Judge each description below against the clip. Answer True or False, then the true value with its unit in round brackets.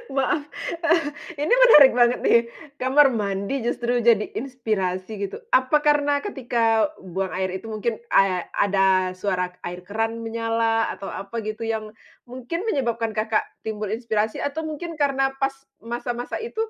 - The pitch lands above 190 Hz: True (230 Hz)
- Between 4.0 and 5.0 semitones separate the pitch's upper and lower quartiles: True (4.4 semitones)